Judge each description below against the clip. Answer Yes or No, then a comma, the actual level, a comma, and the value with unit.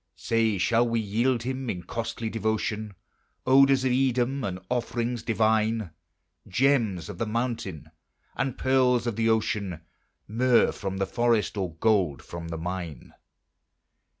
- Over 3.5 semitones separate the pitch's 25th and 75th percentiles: Yes, average, 3.9 semitones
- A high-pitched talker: No, low, 115 Hz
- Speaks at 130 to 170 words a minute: Yes, slow, 135 wpm